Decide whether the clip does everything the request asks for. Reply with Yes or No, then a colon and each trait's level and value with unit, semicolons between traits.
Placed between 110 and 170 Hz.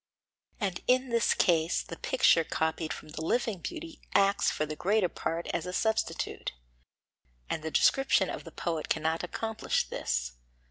No: medium, 180 Hz